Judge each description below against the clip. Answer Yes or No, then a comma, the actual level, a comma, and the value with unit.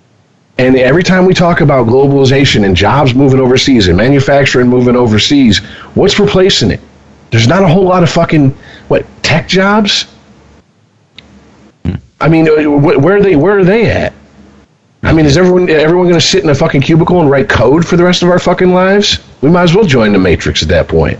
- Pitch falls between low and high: Yes, medium, 150 Hz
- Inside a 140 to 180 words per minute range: No, average, 195 wpm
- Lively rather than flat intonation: Yes, wide, 5.8 semitones